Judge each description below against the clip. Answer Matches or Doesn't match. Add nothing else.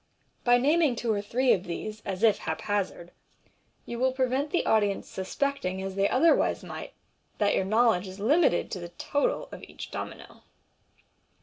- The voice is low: Doesn't match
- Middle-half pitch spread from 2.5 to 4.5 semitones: Doesn't match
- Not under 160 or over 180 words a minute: Matches